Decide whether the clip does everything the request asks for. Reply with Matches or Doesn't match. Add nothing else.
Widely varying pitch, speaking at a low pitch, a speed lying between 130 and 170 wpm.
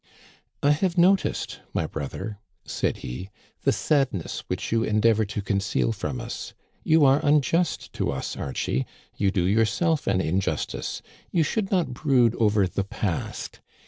Matches